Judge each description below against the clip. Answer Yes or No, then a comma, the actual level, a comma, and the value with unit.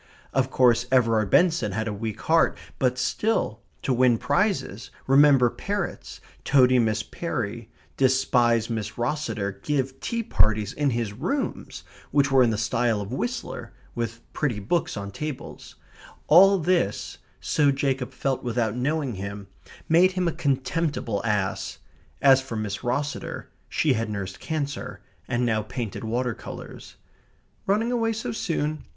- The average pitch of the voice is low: Yes, low, 125 Hz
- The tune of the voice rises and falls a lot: No, average, 5.0 semitones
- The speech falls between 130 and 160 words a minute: Yes, average, 145 wpm